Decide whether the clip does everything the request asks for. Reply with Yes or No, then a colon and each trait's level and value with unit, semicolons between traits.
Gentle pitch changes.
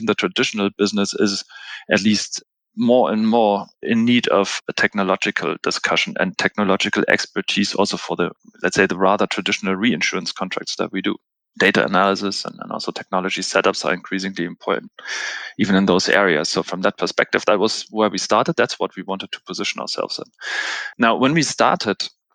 Yes: narrow, 1.9 semitones